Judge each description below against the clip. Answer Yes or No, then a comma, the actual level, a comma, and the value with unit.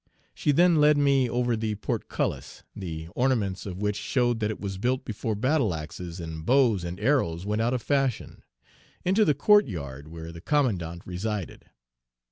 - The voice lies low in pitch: Yes, low, 110 Hz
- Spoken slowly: No, average, 170 wpm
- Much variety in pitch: Yes, wide, 6.9 semitones